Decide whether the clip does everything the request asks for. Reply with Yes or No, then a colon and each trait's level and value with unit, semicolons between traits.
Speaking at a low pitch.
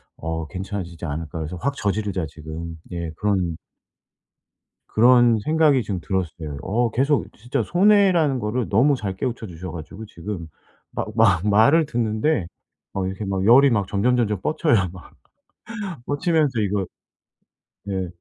Yes: low, 105 Hz